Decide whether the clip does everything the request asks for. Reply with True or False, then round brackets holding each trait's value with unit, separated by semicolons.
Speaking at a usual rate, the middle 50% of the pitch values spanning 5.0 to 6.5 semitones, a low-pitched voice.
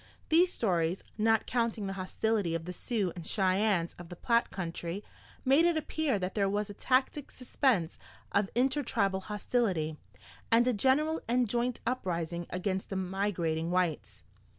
False (150 wpm; 5.3 semitones; 200 Hz)